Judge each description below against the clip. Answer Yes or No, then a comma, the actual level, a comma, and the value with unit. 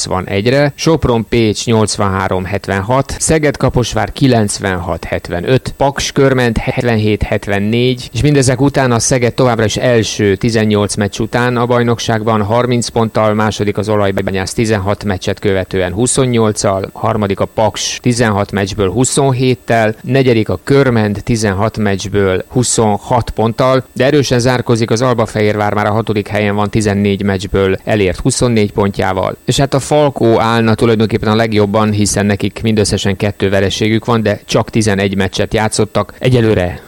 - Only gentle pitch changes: No, average, 3.4 semitones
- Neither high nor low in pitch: No, low, 110 Hz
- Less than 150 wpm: Yes, average, 130 wpm